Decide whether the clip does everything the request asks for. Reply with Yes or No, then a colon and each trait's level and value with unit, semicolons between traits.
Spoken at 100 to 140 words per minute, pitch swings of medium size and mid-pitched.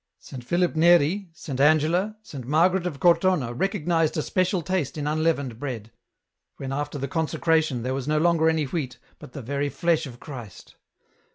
No: average, 175 wpm; average, 3.9 semitones; medium, 155 Hz